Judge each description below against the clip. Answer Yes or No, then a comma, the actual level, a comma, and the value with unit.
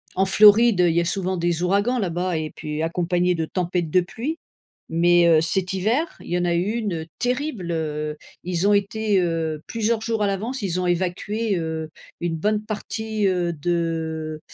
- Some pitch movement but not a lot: Yes, average, 3.9 semitones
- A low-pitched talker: No, medium, 180 Hz